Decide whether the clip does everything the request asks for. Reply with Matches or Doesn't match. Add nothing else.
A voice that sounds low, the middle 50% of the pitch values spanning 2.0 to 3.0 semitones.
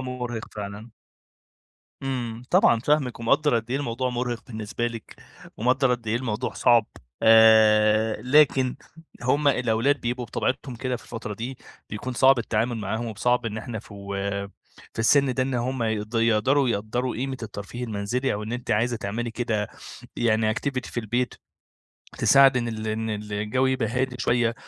Matches